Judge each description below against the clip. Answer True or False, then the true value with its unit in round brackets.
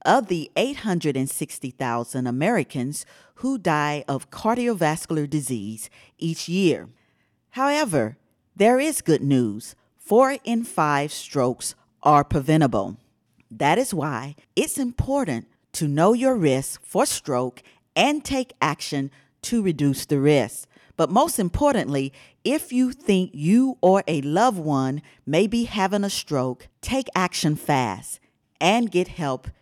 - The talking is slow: True (125 wpm)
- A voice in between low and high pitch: True (155 Hz)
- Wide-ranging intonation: True (9.0 semitones)